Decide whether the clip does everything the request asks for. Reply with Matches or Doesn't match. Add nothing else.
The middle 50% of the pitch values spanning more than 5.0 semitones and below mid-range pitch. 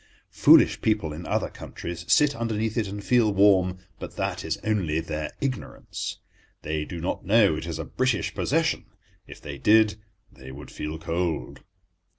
Matches